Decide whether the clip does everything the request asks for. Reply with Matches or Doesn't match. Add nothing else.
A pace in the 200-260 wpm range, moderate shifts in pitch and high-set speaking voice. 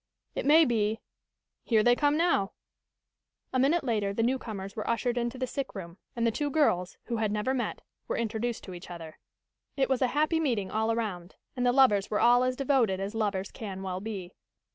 Matches